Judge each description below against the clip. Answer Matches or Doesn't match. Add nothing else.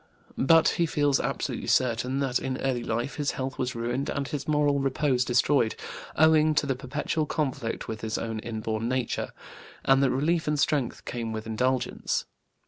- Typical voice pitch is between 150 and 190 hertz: Doesn't match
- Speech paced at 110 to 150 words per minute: Doesn't match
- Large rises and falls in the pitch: Doesn't match